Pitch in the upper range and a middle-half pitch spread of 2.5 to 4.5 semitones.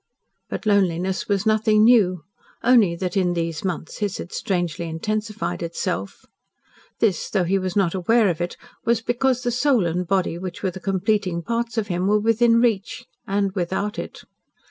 Yes: high, 195 Hz; average, 3.7 semitones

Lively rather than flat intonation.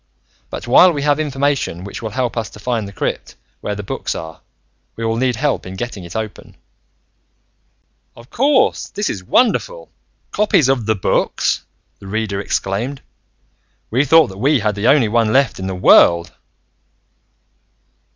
Yes: wide, 5.7 semitones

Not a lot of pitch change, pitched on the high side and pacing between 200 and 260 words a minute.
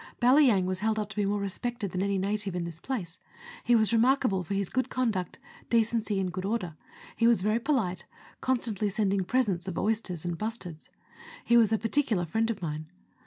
No: average, 3.8 semitones; high, 210 Hz; fast, 205 wpm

